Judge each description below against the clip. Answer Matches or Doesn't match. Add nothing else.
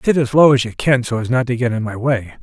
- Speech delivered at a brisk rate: Matches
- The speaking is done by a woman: Doesn't match